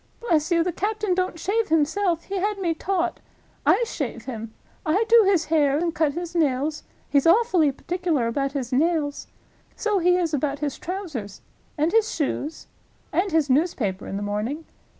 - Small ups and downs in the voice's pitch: No, average, 4.3 semitones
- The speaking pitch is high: Yes, very high, 325 Hz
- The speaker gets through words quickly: No, average, 170 wpm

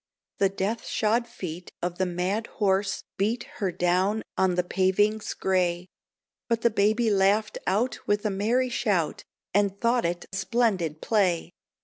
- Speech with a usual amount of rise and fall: Yes, average, 3.2 semitones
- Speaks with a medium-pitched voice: No, high, 200 Hz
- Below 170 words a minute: Yes, average, 145 wpm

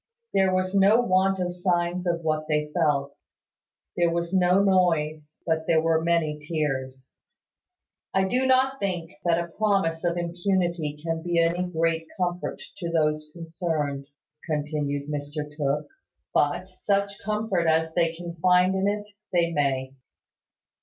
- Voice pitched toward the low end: No, medium, 170 Hz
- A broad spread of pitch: No, average, 3.2 semitones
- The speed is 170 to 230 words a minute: No, average, 145 wpm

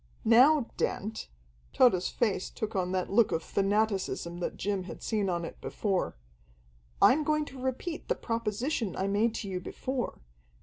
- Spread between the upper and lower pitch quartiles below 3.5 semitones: No, average, 4.5 semitones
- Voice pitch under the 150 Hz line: No, high, 210 Hz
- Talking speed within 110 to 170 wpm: Yes, average, 160 wpm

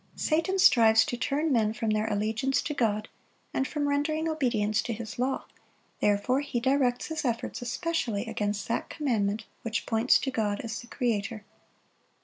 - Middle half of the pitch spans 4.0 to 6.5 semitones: Yes, average, 4.3 semitones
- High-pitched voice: Yes, high, 235 Hz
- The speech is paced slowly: No, average, 160 wpm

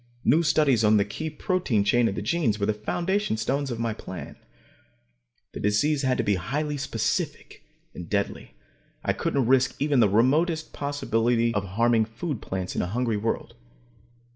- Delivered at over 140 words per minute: Yes, average, 170 wpm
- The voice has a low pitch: Yes, low, 120 Hz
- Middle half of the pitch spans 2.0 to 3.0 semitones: No, wide, 5.5 semitones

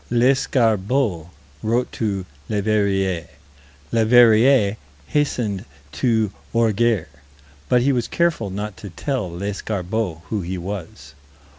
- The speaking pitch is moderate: No, low, 110 Hz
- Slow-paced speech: Yes, slow, 100 wpm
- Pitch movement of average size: Yes, average, 3.9 semitones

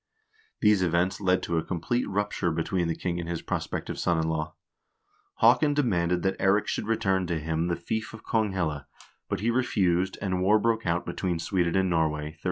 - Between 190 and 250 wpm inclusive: Yes, average, 195 wpm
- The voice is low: Yes, very low, 90 Hz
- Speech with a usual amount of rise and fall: Yes, average, 3.6 semitones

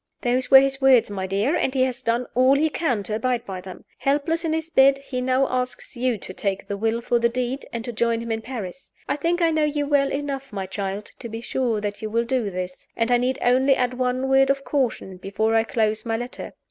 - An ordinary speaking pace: No, fast, 250 wpm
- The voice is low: No, very high, 250 Hz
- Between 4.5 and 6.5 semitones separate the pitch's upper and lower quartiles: No, average, 3.4 semitones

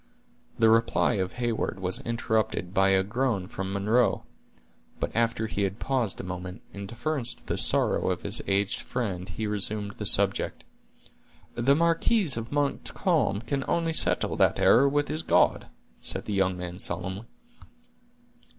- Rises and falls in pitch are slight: No, average, 4.4 semitones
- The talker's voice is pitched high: No, low, 110 Hz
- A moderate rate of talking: Yes, average, 155 wpm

